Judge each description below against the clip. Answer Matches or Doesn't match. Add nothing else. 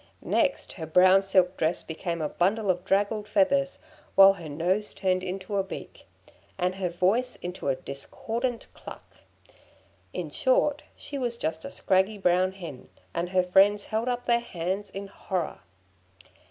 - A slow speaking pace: Doesn't match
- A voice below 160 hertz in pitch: Doesn't match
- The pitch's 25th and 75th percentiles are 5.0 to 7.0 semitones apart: Doesn't match